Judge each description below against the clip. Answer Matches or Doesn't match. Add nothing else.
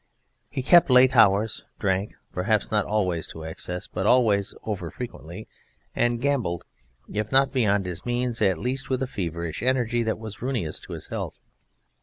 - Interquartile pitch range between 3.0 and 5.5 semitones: Matches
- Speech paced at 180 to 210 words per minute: Doesn't match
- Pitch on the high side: Doesn't match